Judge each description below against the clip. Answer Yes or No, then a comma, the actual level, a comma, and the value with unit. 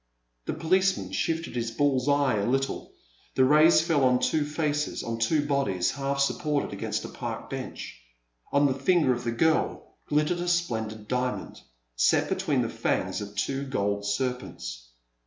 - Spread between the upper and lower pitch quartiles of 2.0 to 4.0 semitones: No, average, 4.8 semitones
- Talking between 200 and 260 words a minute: No, average, 170 wpm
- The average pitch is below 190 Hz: Yes, low, 135 Hz